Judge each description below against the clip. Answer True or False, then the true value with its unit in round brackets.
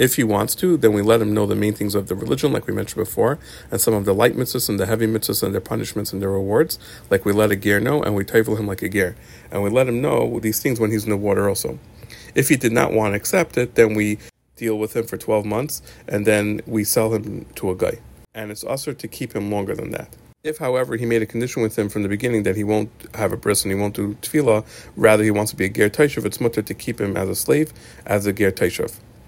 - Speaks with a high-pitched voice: False (110 Hz)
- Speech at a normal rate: False (280 wpm)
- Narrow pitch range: True (2.3 semitones)